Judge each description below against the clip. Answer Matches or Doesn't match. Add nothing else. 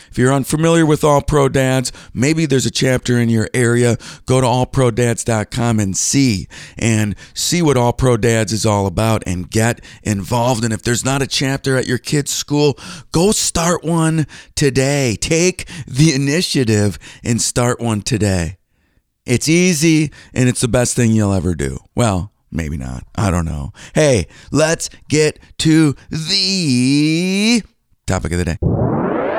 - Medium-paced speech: Matches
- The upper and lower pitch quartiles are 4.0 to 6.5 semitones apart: Matches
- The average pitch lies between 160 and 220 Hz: Doesn't match